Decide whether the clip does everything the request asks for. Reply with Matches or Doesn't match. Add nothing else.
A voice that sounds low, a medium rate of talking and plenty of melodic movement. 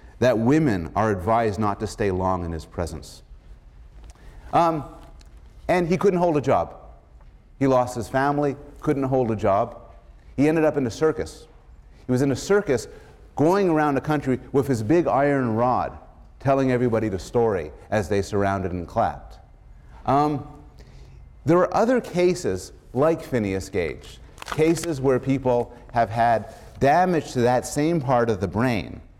Matches